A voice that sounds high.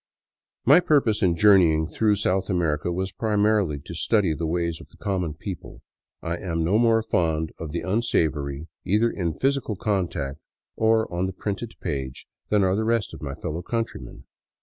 No: very low, 95 Hz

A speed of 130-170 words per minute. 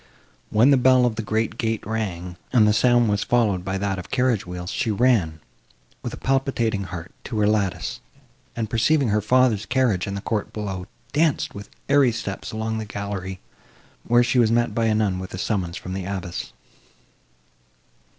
No: average, 185 wpm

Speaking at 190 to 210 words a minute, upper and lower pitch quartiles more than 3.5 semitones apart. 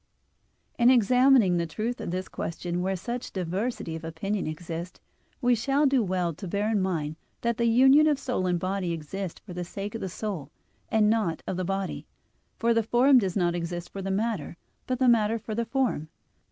Yes: average, 200 wpm; average, 5.1 semitones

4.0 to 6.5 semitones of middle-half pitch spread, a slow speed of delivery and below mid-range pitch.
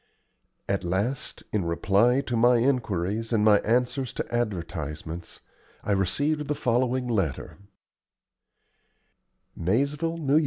Yes: average, 5.1 semitones; slow, 110 wpm; low, 115 Hz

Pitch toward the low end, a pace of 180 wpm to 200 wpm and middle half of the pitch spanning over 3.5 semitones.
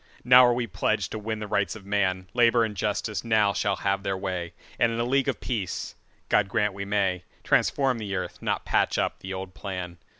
No: low, 100 Hz; average, 195 wpm; average, 3.2 semitones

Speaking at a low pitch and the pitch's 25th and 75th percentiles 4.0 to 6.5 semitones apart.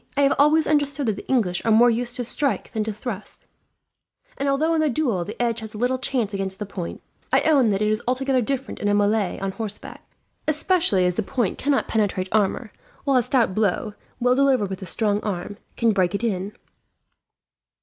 No: high, 225 Hz; average, 4.7 semitones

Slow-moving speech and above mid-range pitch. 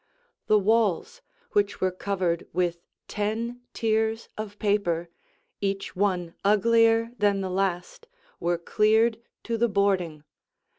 Yes: slow, 115 wpm; high, 205 Hz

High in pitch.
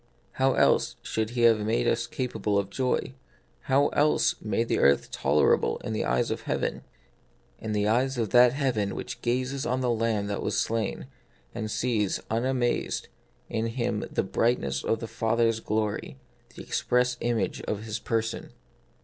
No: low, 115 Hz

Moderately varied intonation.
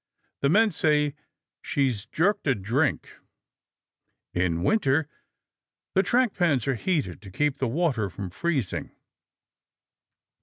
No: wide, 7.8 semitones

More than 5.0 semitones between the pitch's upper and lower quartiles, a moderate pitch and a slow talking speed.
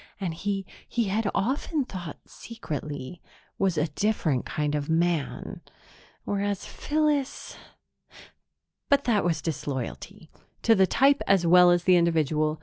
Yes: wide, 5.4 semitones; medium, 180 Hz; slow, 130 wpm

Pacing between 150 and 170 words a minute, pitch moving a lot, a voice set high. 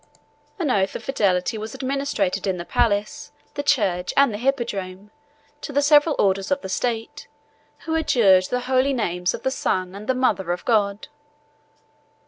Yes: average, 160 wpm; wide, 6.0 semitones; high, 220 Hz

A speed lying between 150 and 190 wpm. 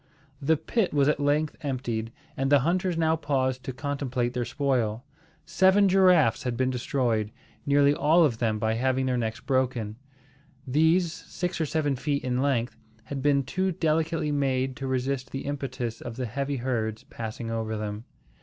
Yes: average, 170 wpm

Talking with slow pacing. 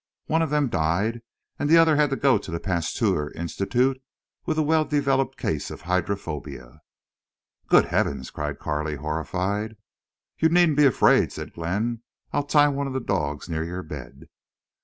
No: average, 165 wpm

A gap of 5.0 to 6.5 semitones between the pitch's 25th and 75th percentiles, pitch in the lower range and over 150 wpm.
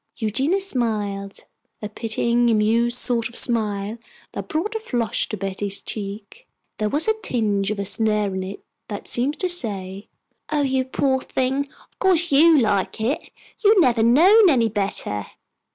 No: wide, 5.5 semitones; high, 230 Hz; average, 165 wpm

